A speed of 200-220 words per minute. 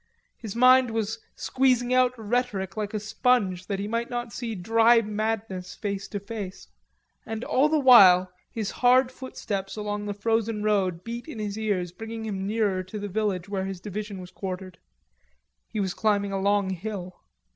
No: average, 175 wpm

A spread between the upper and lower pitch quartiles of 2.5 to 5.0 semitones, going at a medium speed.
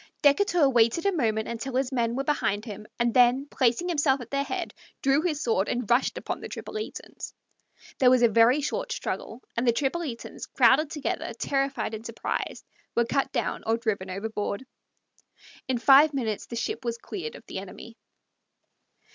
Yes: average, 3.4 semitones; average, 170 wpm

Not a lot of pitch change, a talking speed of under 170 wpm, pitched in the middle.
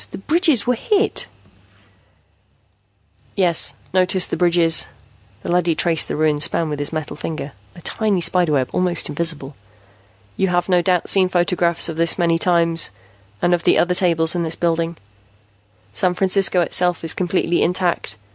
Yes: narrow, 1.8 semitones; average, 160 wpm; medium, 175 Hz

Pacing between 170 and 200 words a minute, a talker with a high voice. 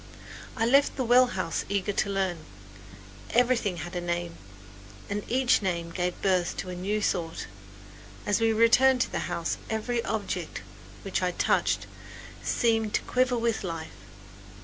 No: average, 150 wpm; high, 200 Hz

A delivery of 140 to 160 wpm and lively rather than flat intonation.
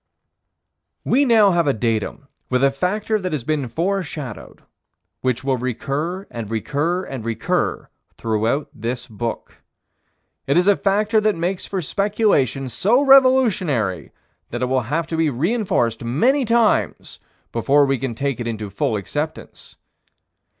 Yes: average, 145 wpm; wide, 8.6 semitones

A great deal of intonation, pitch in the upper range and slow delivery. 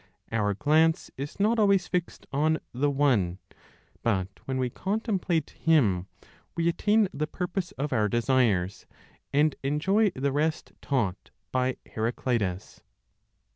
No: wide, 6.5 semitones; medium, 140 Hz; slow, 125 wpm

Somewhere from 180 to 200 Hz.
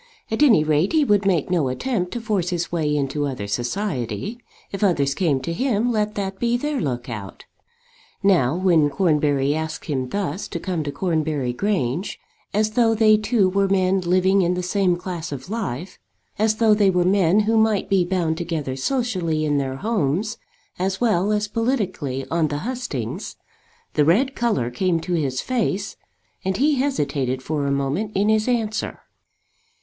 Yes: medium, 185 Hz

